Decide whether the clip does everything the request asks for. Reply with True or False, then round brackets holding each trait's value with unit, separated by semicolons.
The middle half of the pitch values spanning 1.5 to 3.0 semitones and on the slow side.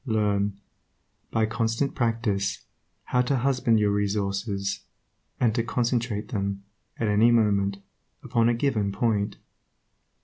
True (2.7 semitones; 115 wpm)